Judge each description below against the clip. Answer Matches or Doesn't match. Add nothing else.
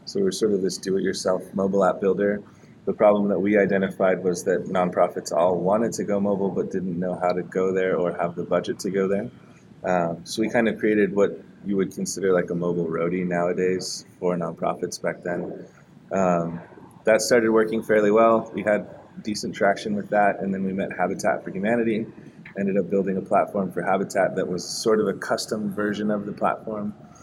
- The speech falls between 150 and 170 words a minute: Doesn't match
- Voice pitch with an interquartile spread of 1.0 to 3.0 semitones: Matches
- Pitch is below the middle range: Matches